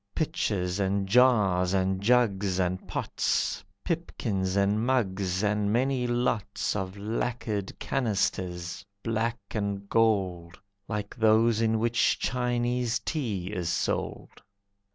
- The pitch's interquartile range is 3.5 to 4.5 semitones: Yes, average, 3.8 semitones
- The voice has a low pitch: Yes, low, 105 Hz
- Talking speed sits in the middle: No, slow, 110 wpm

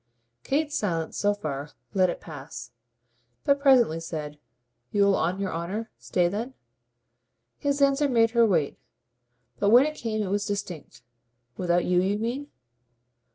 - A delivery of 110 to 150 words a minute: Yes, average, 145 wpm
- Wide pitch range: Yes, wide, 5.8 semitones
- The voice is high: Yes, high, 200 Hz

